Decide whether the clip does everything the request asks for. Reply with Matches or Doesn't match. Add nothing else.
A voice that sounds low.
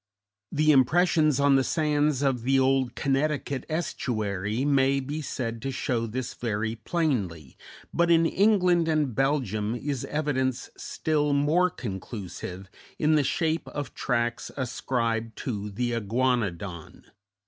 Matches